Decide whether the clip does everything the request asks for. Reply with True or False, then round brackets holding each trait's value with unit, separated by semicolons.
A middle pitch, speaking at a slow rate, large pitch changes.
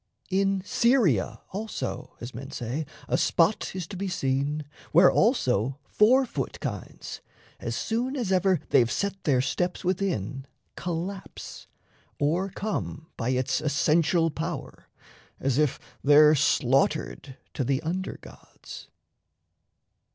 True (160 Hz; 120 wpm; 6.1 semitones)